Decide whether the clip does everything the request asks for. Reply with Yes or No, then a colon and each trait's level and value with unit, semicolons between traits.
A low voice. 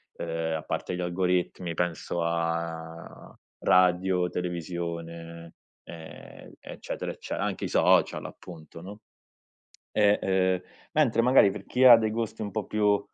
Yes: very low, 90 Hz